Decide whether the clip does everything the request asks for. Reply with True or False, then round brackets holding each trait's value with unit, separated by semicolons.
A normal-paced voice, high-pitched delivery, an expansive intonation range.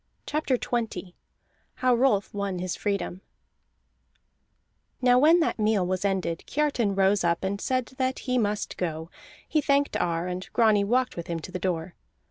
True (160 wpm; 205 Hz; 5.7 semitones)